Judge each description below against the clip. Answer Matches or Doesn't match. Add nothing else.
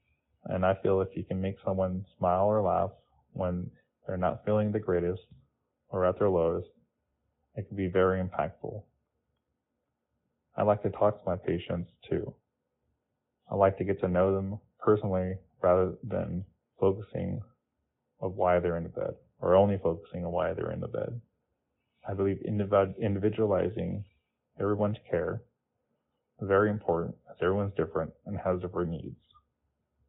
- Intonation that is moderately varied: Doesn't match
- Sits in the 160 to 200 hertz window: Doesn't match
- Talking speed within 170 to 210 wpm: Doesn't match